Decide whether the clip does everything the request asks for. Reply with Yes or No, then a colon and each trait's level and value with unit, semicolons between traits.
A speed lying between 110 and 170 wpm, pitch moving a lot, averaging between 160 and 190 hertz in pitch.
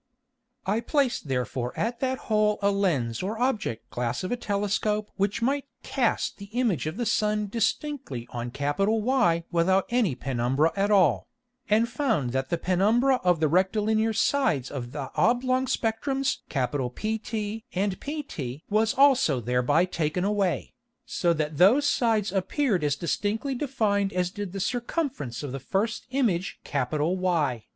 No: average, 145 wpm; wide, 7.3 semitones; high, 200 Hz